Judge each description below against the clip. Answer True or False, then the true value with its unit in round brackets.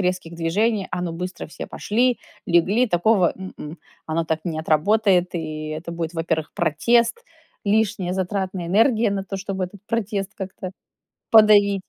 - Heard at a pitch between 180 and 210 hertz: True (185 Hz)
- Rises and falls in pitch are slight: False (3.7 semitones)